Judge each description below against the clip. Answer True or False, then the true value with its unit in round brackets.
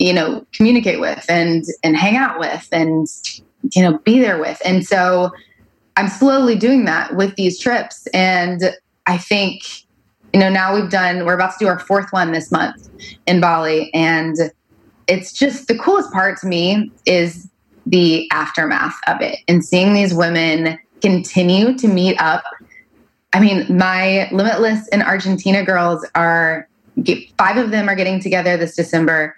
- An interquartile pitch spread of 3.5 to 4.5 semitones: False (3.1 semitones)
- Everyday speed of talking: True (165 wpm)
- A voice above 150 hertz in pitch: True (185 Hz)